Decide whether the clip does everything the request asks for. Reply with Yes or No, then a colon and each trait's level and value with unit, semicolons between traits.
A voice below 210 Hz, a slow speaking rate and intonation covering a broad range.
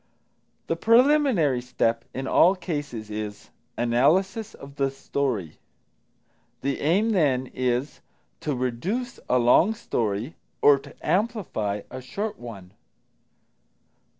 Yes: medium, 140 Hz; slow, 110 wpm; wide, 7.8 semitones